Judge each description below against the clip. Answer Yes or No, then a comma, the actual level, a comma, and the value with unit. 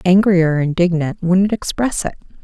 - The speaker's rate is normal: Yes, average, 150 wpm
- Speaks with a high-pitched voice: No, medium, 180 Hz